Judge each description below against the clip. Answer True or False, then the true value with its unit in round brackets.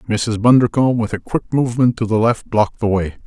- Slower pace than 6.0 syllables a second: False (6.4 syllables/s)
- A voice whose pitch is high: False (115 Hz)